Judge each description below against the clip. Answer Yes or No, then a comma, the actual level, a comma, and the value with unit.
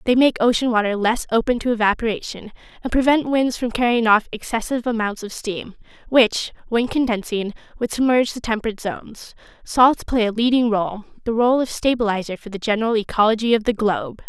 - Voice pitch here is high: Yes, high, 230 Hz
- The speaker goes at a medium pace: Yes, average, 175 wpm